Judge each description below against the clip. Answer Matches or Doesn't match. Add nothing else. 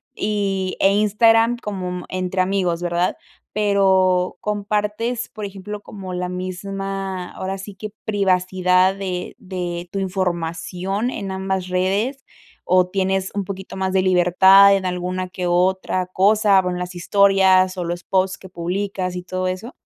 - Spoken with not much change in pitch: Matches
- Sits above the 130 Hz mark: Matches